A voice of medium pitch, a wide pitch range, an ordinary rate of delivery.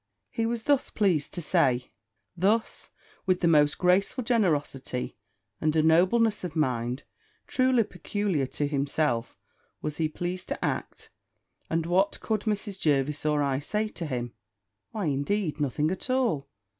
Yes: medium, 165 Hz; wide, 6.0 semitones; average, 145 wpm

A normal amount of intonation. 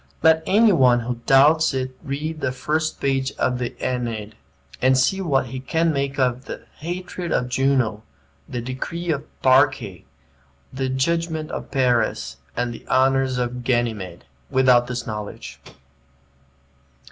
Yes: average, 3.4 semitones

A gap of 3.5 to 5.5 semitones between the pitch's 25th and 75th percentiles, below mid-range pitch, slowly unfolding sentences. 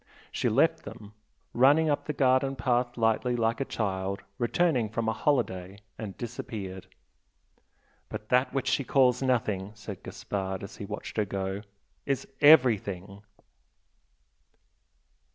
Yes: average, 4.5 semitones; low, 115 Hz; slow, 130 wpm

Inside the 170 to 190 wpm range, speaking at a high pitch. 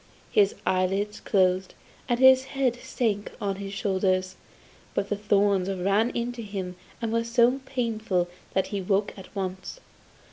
No: average, 145 wpm; high, 200 Hz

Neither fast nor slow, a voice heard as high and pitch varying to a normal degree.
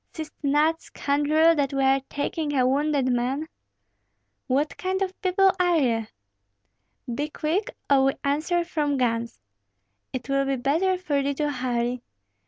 Yes: average, 150 wpm; very high, 285 Hz; average, 3.1 semitones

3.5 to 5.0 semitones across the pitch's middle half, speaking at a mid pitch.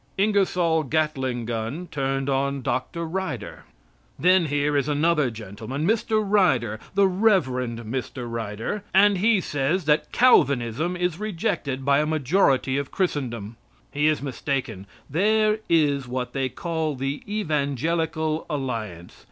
No: wide, 5.5 semitones; medium, 145 Hz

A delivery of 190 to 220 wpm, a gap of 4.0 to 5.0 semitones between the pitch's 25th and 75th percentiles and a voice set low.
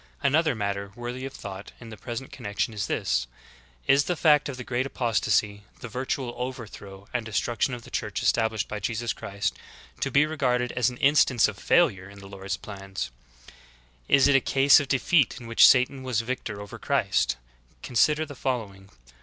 Yes: average, 195 wpm; average, 4.6 semitones; low, 120 Hz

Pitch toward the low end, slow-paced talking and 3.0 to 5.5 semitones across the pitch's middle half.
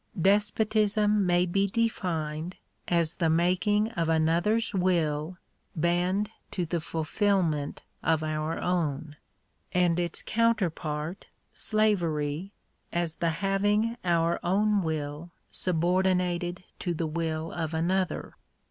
No: medium, 175 Hz; slow, 110 wpm; average, 3.4 semitones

